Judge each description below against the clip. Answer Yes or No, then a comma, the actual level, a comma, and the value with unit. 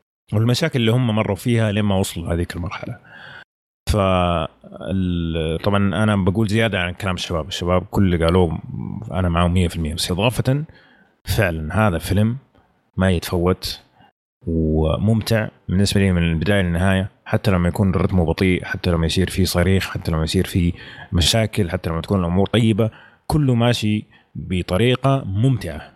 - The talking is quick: Yes, fast, 140 wpm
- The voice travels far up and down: No, average, 3.8 semitones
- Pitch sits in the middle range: No, very low, 95 Hz